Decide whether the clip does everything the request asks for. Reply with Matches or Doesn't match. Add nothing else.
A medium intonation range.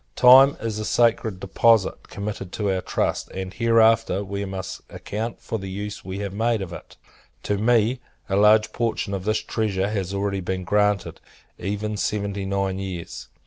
Doesn't match